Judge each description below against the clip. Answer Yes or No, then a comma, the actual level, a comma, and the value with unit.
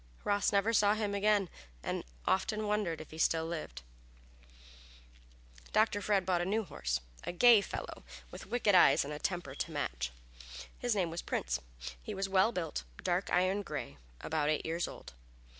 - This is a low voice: No, medium, 185 Hz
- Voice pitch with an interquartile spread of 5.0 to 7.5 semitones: No, average, 4.6 semitones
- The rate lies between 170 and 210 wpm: Yes, average, 175 wpm